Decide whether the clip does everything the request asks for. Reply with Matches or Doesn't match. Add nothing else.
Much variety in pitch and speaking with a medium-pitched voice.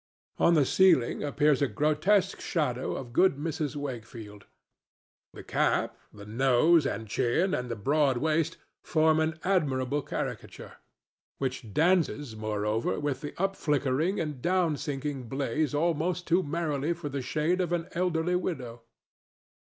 Doesn't match